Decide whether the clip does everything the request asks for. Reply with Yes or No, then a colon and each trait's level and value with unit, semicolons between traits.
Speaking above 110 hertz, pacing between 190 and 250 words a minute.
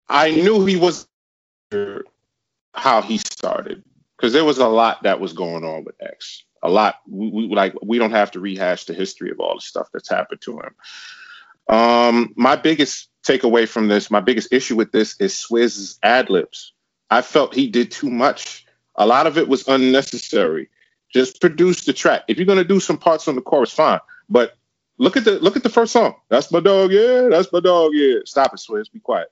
Yes: low, 135 Hz; fast, 205 wpm